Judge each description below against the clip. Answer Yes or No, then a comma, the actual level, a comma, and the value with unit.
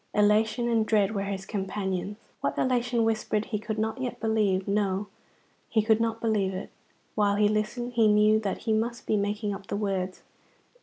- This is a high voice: Yes, high, 210 Hz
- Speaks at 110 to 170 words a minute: No, average, 185 wpm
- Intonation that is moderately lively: No, narrow, 1.8 semitones